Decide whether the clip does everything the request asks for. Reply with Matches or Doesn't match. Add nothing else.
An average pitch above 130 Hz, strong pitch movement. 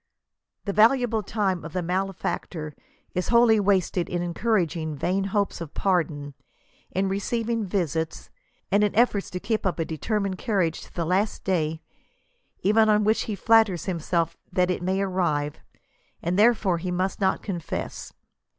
Doesn't match